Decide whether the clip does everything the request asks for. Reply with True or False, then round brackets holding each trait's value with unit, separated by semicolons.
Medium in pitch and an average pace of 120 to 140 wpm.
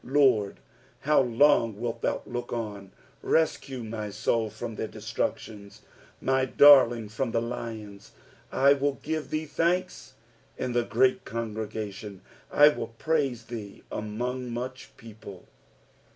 False (115 Hz; 135 wpm)